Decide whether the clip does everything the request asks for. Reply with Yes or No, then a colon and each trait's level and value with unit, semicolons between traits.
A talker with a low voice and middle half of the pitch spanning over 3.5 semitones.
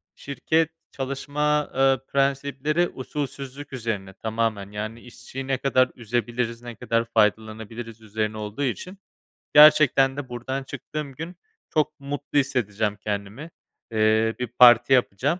Yes: low, 125 Hz; average, 3.9 semitones